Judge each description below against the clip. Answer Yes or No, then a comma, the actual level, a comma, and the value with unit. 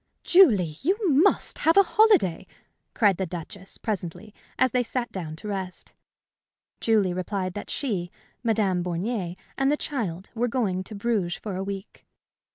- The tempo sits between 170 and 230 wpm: No, average, 155 wpm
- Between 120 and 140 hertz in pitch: No, high, 205 Hz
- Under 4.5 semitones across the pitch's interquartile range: No, average, 5.3 semitones